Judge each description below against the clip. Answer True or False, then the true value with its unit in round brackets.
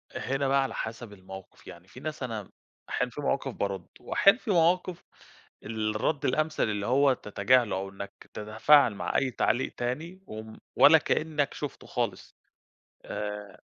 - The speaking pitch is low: True (120 Hz)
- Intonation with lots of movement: True (5.7 semitones)